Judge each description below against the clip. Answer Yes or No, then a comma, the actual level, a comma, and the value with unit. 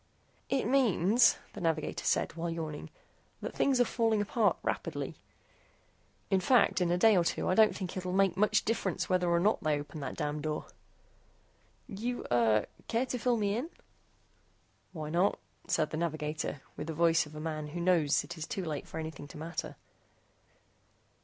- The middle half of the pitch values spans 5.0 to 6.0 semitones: Yes, wide, 5.4 semitones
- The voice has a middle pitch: Yes, medium, 175 Hz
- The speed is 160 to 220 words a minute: Yes, average, 180 wpm